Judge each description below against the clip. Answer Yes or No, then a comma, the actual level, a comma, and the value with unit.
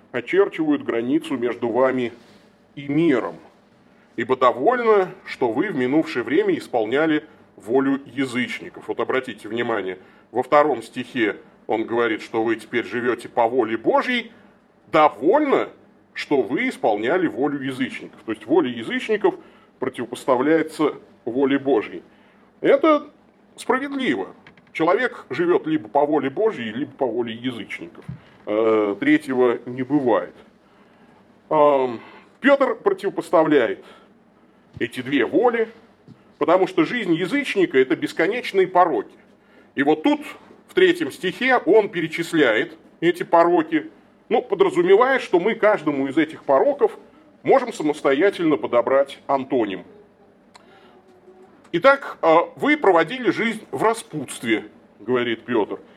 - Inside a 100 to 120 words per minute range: Yes, slow, 110 wpm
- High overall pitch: Yes, high, 210 Hz